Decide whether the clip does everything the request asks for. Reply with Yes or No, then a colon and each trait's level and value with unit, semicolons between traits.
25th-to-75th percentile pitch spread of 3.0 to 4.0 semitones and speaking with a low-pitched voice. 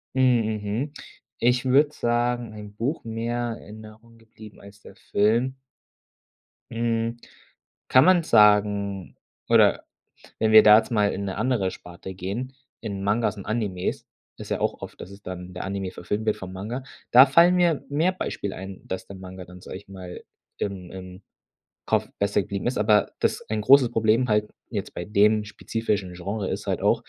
Yes: average, 3.3 semitones; low, 105 Hz